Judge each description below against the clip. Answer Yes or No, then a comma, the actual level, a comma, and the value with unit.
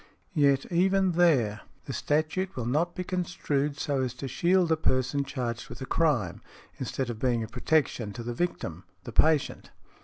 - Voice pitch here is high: No, medium, 140 Hz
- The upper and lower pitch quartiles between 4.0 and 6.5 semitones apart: Yes, average, 5.2 semitones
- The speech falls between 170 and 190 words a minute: Yes, average, 175 wpm